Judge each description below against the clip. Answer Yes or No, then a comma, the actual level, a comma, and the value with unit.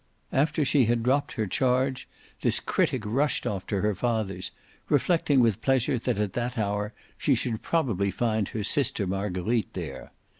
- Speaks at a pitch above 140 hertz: No, low, 115 Hz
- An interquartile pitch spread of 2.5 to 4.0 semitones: No, average, 4.4 semitones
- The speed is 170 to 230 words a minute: No, average, 160 wpm